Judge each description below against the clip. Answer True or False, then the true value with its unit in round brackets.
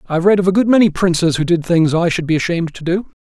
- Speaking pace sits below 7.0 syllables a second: False (7.1 syllables/s)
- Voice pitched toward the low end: False (175 Hz)